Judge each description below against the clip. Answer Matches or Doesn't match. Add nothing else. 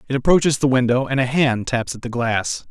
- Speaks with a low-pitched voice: Matches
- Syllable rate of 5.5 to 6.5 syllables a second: Matches